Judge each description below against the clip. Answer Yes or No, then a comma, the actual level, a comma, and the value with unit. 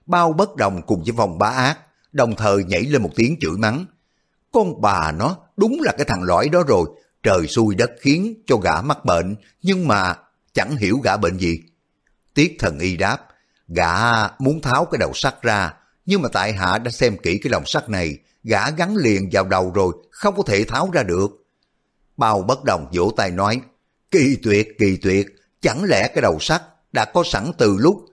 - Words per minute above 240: No, average, 205 wpm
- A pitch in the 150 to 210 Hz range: No, low, 115 Hz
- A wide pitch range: Yes, wide, 7.2 semitones